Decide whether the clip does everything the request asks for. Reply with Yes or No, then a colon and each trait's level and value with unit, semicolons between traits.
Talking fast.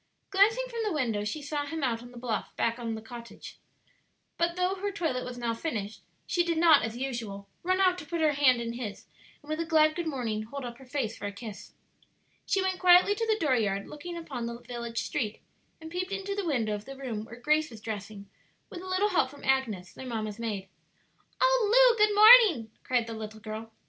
Yes: fast, 220 wpm